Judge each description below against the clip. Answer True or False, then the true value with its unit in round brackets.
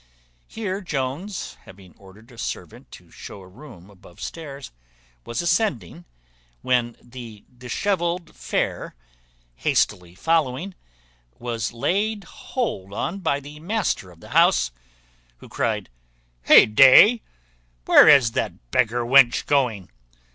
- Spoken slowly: True (115 wpm)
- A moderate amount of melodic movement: False (8.0 semitones)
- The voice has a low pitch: True (130 Hz)